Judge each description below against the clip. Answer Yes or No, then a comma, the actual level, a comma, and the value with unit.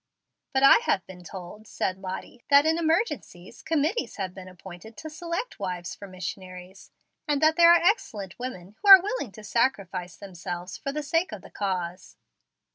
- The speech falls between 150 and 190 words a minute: Yes, average, 175 wpm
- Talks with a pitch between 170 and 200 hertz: No, high, 210 Hz